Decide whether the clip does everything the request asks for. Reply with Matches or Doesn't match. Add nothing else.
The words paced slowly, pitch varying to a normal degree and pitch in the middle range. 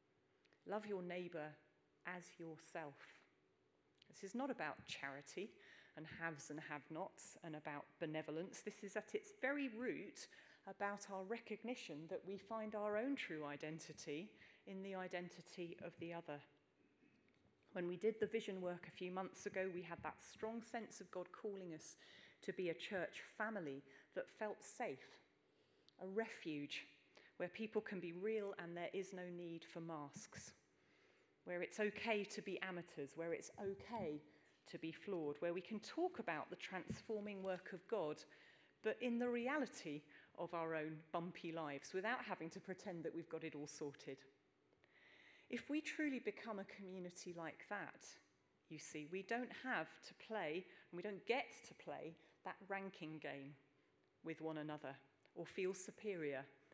Doesn't match